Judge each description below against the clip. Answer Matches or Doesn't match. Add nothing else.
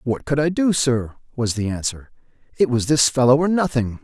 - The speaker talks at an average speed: Doesn't match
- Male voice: Matches